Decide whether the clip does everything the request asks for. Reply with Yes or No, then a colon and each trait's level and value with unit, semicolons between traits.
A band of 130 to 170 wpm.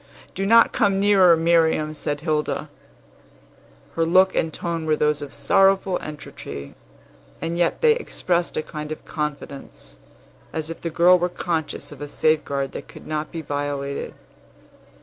Yes: average, 150 wpm